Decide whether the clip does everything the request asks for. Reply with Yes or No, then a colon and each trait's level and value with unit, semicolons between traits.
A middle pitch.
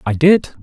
Yes: medium, 145 Hz